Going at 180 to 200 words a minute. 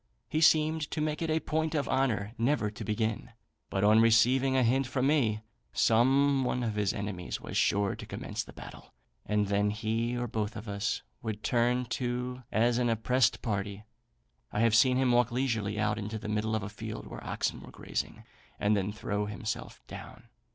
Yes: average, 195 wpm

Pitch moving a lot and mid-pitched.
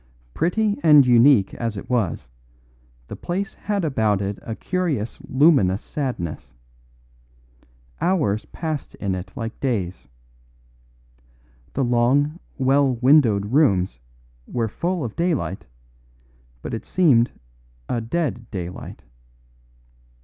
No: wide, 6.9 semitones; low, 125 Hz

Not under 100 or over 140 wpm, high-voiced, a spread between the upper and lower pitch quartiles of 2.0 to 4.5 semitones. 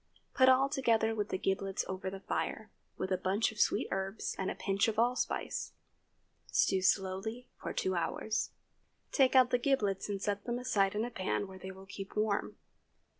No: average, 185 wpm; high, 205 Hz; average, 3.5 semitones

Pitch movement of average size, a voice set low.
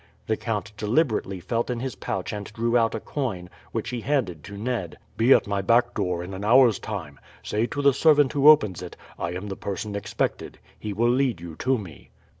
Yes: average, 4.3 semitones; low, 110 Hz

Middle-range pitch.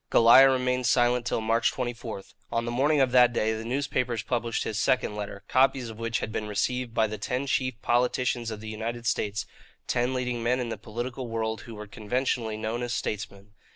No: low, 120 Hz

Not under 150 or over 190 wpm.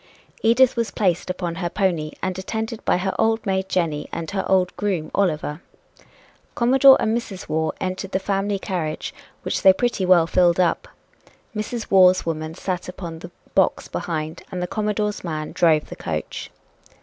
Yes: average, 165 wpm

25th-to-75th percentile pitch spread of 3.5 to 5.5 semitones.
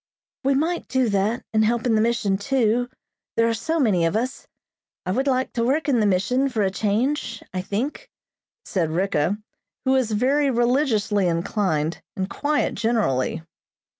Yes: average, 4.8 semitones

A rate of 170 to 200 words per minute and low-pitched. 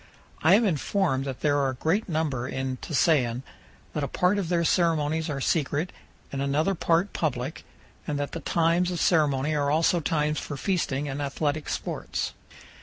No: average, 175 wpm; medium, 150 Hz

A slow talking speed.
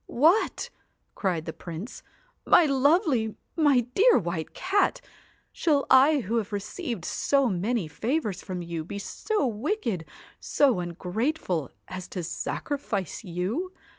Yes: slow, 125 wpm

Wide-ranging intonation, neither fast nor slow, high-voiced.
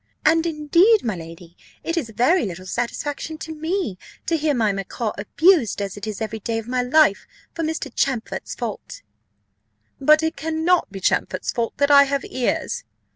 Yes: wide, 6.7 semitones; average, 175 wpm; very high, 275 Hz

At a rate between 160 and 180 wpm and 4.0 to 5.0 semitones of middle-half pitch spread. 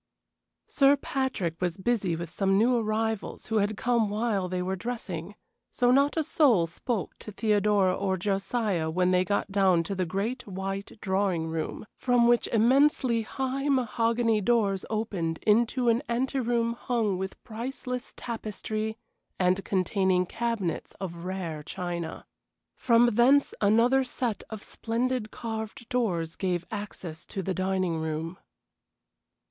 No: average, 140 wpm; average, 4.3 semitones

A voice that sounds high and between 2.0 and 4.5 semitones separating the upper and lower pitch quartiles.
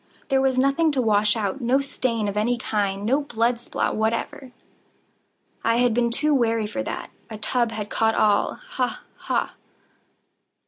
Yes: high, 235 Hz; average, 3.5 semitones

